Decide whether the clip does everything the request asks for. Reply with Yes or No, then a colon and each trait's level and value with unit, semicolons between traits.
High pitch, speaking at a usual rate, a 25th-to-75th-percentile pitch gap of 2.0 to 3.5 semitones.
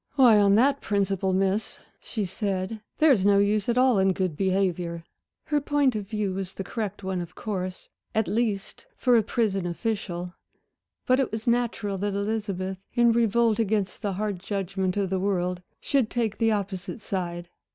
Yes: high, 200 Hz; average, 170 wpm; average, 3.1 semitones